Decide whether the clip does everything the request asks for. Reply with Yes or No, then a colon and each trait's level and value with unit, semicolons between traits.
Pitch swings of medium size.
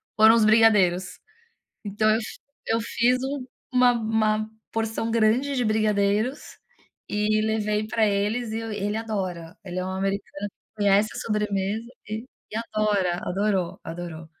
No: narrow, 2.0 semitones